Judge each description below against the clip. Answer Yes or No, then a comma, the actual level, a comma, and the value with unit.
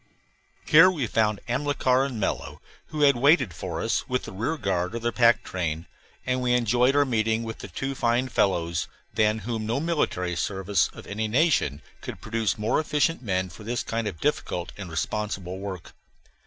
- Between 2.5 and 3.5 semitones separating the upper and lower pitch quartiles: No, average, 4.9 semitones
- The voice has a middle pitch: No, low, 110 Hz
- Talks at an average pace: Yes, average, 180 wpm